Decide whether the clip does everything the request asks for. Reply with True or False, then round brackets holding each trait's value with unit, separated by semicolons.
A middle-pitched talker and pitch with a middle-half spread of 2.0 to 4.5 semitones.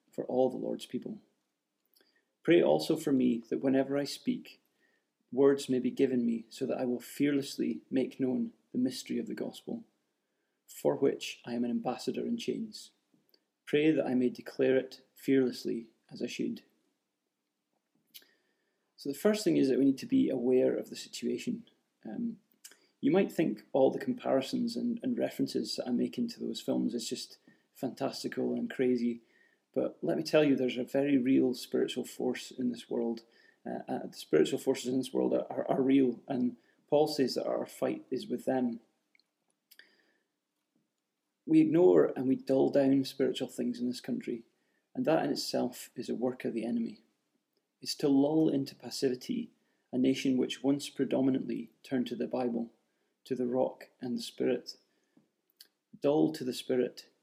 False (130 Hz; 2.6 semitones)